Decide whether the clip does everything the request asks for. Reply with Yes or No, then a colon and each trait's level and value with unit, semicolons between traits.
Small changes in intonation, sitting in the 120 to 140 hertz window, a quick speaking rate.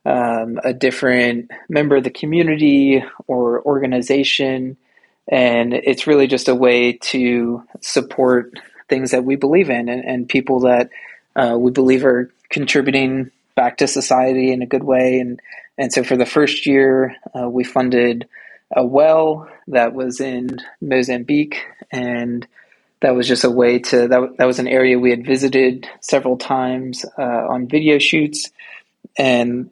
No: narrow, 1.5 semitones; low, 130 Hz; average, 155 wpm